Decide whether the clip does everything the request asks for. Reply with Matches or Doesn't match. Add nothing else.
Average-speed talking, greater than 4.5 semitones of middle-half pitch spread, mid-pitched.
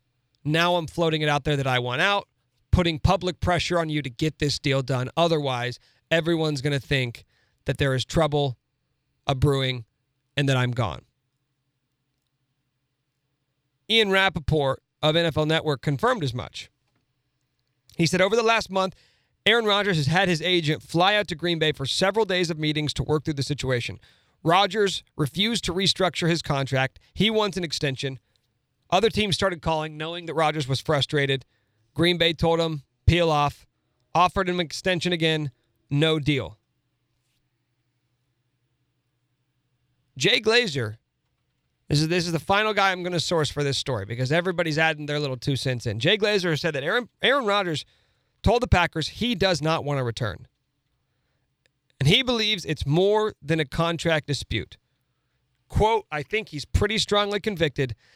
Matches